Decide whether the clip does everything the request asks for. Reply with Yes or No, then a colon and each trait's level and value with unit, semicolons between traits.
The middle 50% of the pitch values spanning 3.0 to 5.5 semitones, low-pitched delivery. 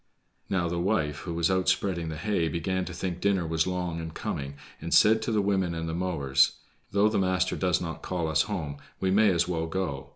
No: narrow, 2.5 semitones; very low, 90 Hz